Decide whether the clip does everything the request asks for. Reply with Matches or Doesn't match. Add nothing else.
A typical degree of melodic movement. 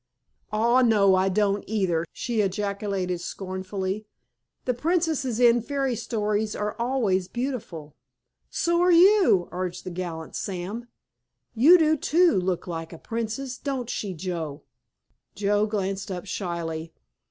Matches